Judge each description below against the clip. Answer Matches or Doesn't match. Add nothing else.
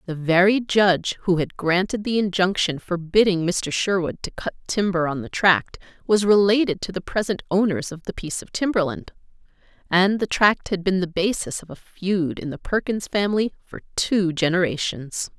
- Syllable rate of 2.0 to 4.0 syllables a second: Doesn't match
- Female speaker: Matches